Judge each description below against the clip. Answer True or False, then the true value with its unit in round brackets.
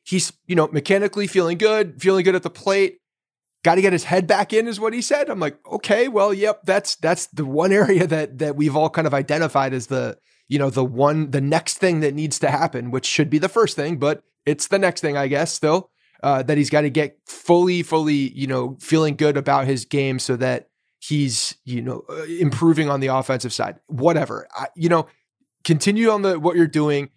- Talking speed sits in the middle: False (225 wpm)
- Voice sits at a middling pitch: True (155 Hz)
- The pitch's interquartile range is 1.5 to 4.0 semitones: False (4.6 semitones)